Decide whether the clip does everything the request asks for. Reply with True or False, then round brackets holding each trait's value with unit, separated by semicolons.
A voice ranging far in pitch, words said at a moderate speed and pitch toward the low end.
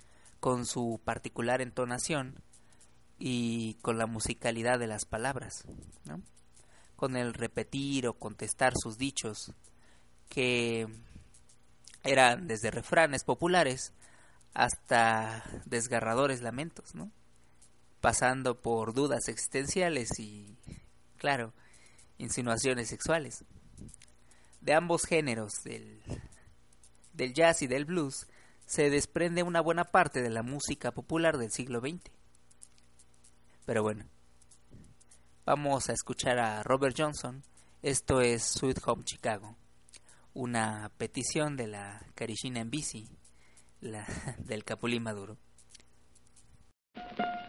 False (7.6 semitones; 100 wpm; 115 Hz)